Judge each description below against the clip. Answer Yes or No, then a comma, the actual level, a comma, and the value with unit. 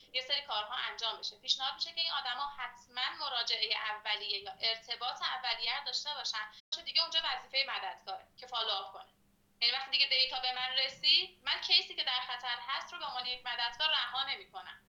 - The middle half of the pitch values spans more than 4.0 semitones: No, average, 3.3 semitones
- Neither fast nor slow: No, fast, 185 wpm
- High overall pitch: Yes, very high, 250 Hz